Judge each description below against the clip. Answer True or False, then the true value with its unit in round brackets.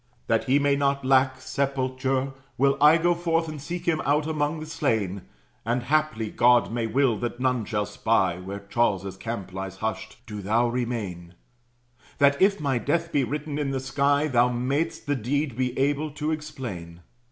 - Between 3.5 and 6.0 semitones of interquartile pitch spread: True (4.4 semitones)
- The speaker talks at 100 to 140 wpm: False (175 wpm)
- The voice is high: False (130 Hz)